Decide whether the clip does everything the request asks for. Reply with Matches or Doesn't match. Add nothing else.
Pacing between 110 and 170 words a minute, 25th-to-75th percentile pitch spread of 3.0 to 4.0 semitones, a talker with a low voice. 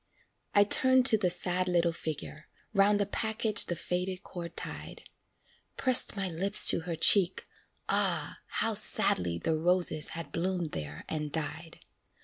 Doesn't match